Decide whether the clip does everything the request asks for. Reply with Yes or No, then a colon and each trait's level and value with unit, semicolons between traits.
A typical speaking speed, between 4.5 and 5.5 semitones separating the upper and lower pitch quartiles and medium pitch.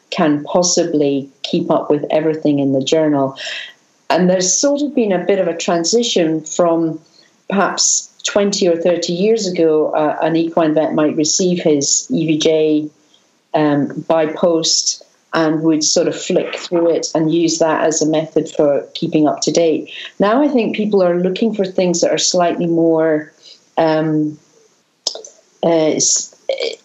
No: average, 155 wpm; narrow, 2.6 semitones; medium, 165 Hz